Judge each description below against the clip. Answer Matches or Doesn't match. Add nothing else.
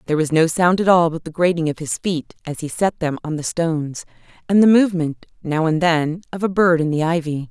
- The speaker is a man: Doesn't match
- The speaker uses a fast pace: Matches